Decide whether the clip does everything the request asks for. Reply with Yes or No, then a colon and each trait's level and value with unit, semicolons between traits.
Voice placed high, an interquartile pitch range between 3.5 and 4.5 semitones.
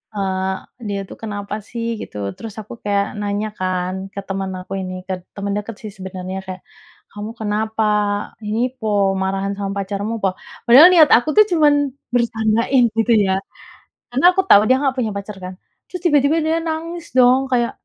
Yes: high, 210 Hz; average, 4.0 semitones